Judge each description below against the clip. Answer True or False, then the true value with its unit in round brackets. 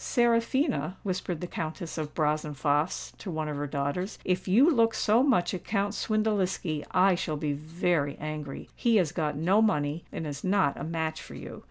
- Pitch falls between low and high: True (170 Hz)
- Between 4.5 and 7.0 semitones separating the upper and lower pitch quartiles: True (5.1 semitones)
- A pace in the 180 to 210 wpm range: True (185 wpm)